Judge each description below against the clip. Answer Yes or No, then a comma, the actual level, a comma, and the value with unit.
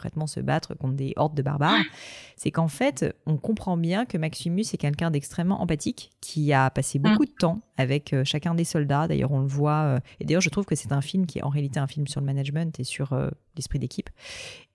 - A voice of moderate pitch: Yes, medium, 155 Hz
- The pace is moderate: No, fast, 225 wpm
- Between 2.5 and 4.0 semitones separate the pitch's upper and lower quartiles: Yes, average, 3.7 semitones